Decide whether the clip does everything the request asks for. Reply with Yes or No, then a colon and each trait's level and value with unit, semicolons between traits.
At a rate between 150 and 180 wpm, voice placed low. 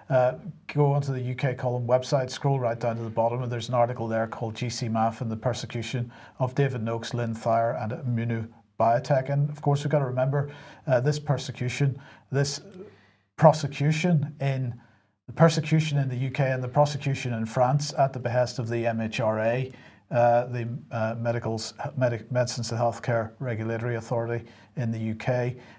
Yes: average, 170 wpm; low, 125 Hz